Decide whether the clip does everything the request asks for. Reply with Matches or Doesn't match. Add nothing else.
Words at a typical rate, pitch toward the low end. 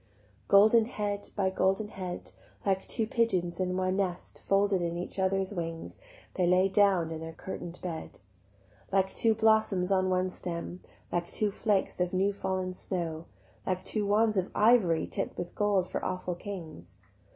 Doesn't match